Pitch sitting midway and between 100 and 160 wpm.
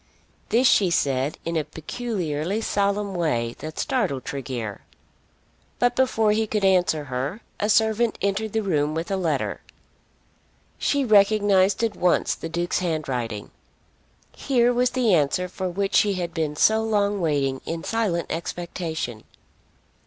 Yes: medium, 180 Hz; average, 140 wpm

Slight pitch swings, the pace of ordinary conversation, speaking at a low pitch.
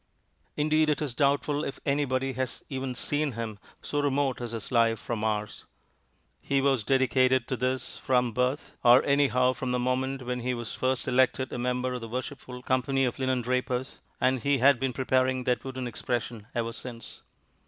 Yes: narrow, 1.6 semitones; average, 175 wpm; low, 130 Hz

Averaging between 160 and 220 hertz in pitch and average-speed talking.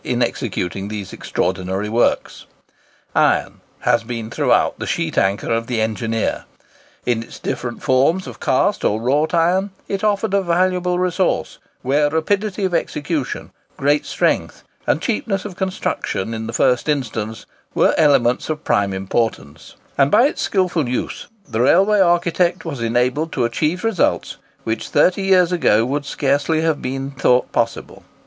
No: medium, 145 Hz; average, 150 wpm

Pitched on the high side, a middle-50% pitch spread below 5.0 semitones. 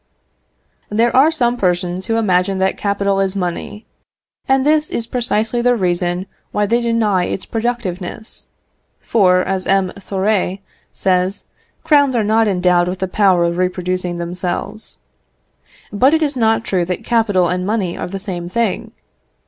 Yes: high, 195 Hz; average, 4.0 semitones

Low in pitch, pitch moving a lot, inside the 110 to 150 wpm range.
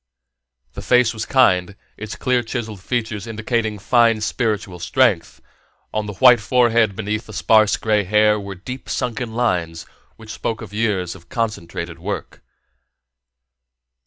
No: low, 110 Hz; average, 2.8 semitones; slow, 135 wpm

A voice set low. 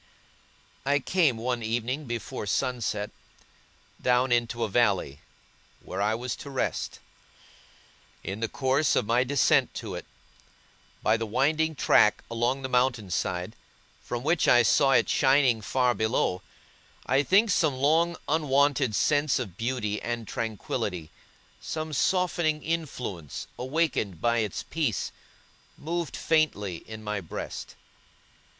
Yes: low, 125 Hz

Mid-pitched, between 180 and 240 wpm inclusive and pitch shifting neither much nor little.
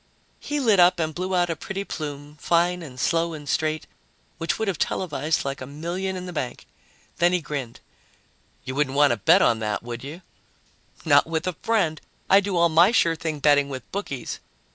Yes: medium, 160 Hz; average, 200 wpm; average, 4.0 semitones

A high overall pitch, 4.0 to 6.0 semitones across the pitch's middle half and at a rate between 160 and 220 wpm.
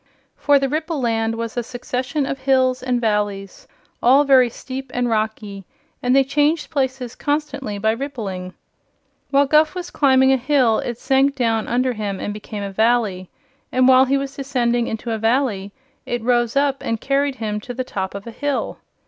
No: very high, 250 Hz; average, 3.5 semitones; average, 180 wpm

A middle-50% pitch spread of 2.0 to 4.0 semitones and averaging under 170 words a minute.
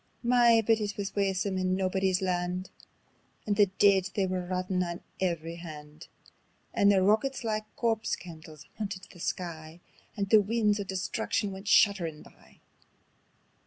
Yes: narrow, 2.6 semitones; average, 150 wpm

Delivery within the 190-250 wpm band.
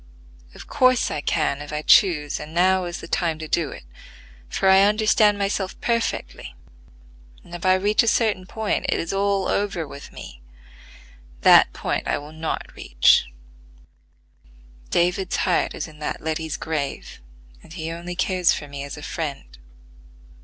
No: average, 160 wpm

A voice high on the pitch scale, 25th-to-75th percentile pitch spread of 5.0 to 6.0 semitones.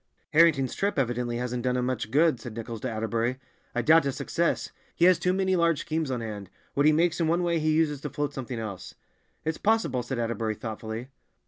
No: low, 130 Hz; wide, 5.6 semitones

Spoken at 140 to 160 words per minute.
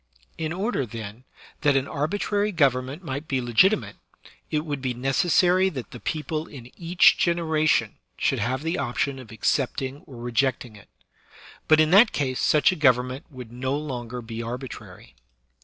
No: average, 170 wpm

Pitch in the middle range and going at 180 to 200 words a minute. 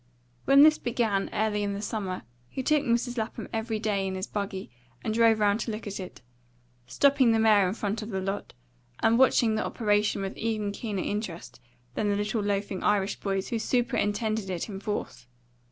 No: high, 210 Hz; average, 190 wpm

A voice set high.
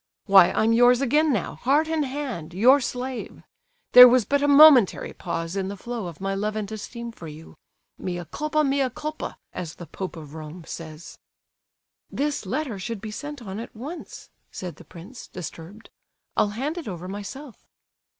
Yes: high, 225 Hz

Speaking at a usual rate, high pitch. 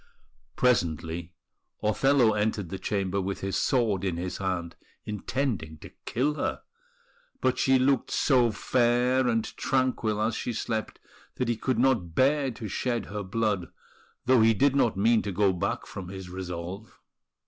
No: average, 155 wpm; low, 110 Hz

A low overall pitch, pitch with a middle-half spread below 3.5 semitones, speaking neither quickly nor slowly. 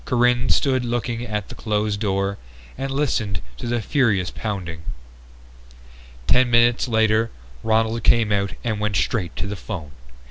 Yes: low, 110 Hz; average, 3.1 semitones; average, 145 wpm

